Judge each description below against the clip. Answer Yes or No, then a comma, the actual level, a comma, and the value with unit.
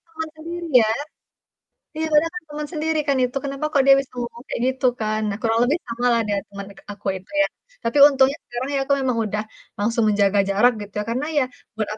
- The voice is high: Yes, high, 245 Hz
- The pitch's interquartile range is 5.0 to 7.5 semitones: Yes, wide, 5.4 semitones